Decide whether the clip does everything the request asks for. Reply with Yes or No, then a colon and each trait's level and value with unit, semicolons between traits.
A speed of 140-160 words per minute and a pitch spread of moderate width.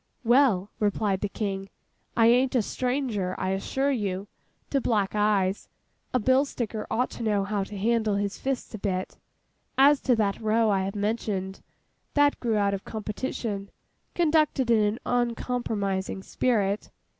Yes: average, 155 wpm; average, 3.8 semitones